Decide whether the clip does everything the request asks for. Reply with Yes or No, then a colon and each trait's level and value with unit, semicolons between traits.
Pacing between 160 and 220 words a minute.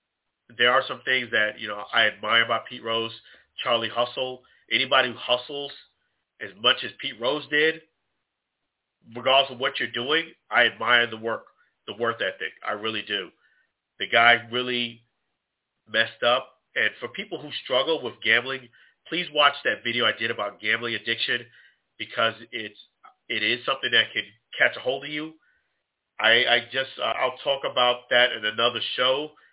Yes: average, 165 wpm